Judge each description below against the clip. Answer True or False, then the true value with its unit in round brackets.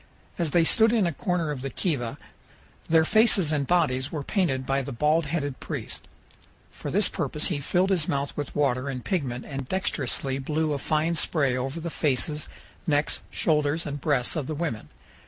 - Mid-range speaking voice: True (150 Hz)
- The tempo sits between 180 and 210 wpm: True (185 wpm)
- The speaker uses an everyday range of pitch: True (3.5 semitones)